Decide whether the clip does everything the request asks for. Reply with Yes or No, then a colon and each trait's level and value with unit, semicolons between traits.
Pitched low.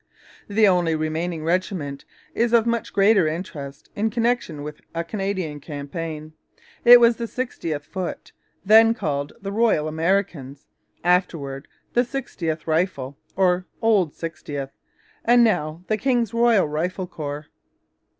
No: medium, 180 Hz